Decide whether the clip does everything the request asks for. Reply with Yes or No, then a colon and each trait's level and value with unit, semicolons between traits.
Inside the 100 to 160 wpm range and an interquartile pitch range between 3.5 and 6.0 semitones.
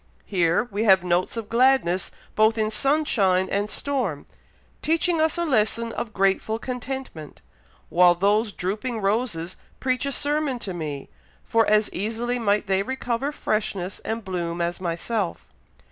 Yes: average, 145 wpm; average, 5.1 semitones